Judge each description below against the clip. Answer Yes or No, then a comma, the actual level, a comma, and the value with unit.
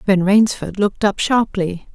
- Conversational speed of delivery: Yes, average, 155 wpm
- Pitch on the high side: Yes, high, 200 Hz